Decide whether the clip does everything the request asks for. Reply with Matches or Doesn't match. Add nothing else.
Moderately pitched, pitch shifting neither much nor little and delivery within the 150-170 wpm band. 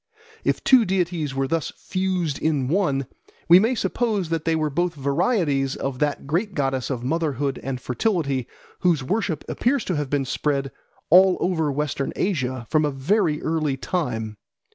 Matches